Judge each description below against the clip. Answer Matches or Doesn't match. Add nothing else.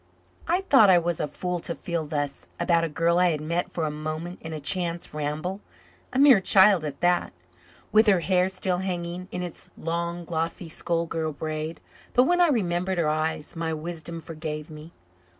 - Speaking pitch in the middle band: Matches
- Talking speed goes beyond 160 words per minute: Matches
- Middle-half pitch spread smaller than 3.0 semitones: Matches